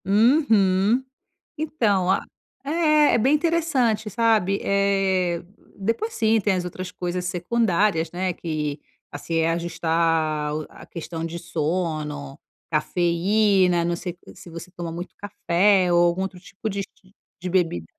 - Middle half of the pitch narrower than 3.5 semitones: No, average, 3.8 semitones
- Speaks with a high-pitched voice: No, medium, 180 Hz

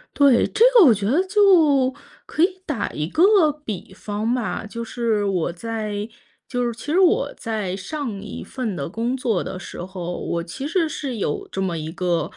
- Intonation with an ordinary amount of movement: No, wide, 7.4 semitones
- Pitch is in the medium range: No, high, 230 Hz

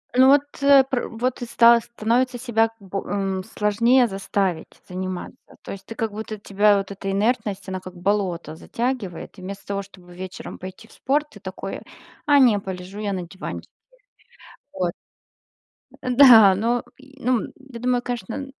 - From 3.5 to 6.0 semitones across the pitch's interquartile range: Yes, average, 4.2 semitones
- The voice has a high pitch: Yes, high, 210 Hz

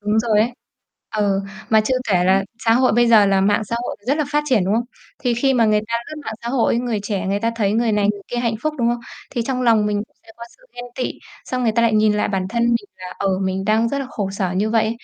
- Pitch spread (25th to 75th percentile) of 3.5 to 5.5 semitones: No, average, 2.7 semitones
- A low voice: No, high, 220 Hz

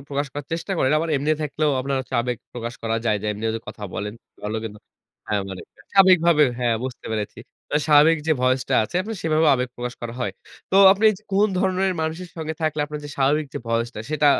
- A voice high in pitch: No, medium, 145 Hz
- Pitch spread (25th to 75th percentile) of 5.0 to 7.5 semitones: Yes, average, 5.3 semitones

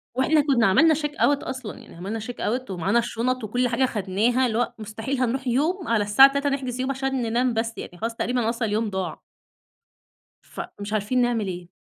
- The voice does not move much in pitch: No, average, 3.4 semitones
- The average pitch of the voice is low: No, high, 240 Hz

